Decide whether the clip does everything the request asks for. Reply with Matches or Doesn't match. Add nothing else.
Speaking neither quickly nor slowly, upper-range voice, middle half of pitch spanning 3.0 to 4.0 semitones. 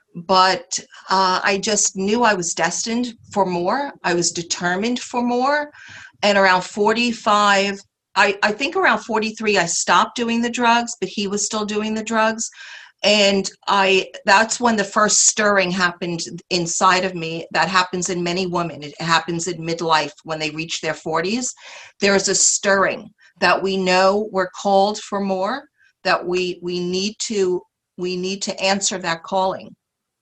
Matches